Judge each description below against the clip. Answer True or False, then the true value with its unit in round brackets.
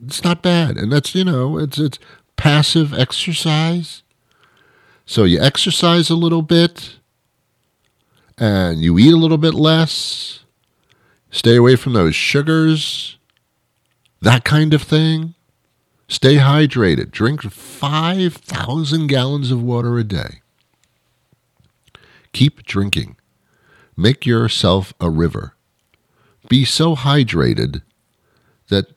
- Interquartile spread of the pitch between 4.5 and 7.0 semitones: True (5.4 semitones)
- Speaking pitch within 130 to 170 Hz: True (140 Hz)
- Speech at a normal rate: False (110 wpm)